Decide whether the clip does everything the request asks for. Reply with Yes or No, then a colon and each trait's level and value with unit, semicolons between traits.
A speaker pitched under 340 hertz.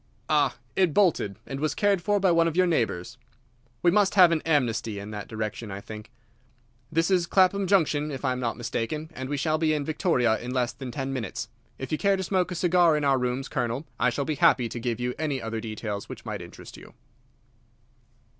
Yes: medium, 140 Hz